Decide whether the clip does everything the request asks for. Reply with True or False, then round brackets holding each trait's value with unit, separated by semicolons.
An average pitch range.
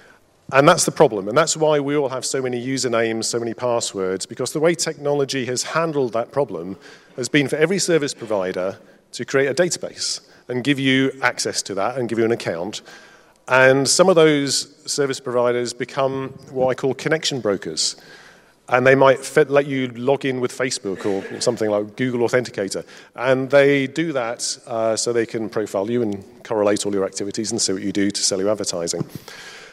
True (3.5 semitones)